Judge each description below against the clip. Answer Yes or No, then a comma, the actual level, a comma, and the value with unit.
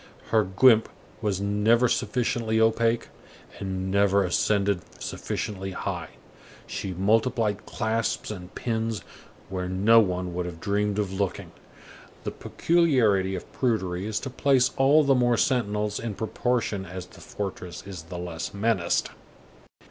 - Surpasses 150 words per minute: No, slow, 135 wpm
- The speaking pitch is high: No, low, 105 Hz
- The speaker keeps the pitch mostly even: No, average, 3.3 semitones